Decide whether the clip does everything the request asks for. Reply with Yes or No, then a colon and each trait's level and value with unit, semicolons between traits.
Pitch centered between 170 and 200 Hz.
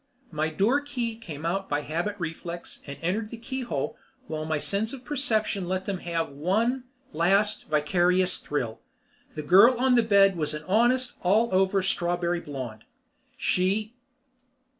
Yes: medium, 185 Hz